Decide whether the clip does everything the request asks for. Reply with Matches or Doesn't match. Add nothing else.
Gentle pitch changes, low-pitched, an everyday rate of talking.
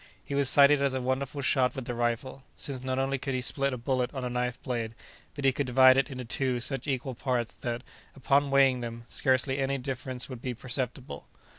Doesn't match